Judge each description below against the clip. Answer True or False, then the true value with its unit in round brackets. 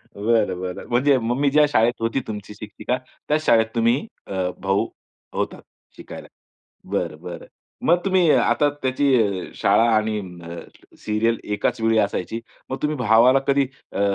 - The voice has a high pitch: False (115 Hz)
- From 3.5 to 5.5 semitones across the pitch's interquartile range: True (4.6 semitones)